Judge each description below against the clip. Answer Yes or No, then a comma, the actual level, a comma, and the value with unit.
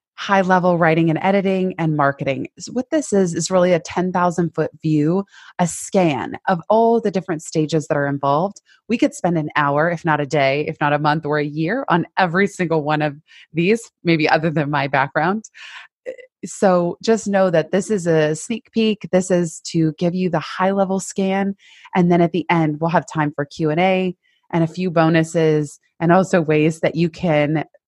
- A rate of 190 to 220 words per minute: Yes, average, 200 wpm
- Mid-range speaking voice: Yes, medium, 170 Hz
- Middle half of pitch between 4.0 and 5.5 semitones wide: No, average, 3.4 semitones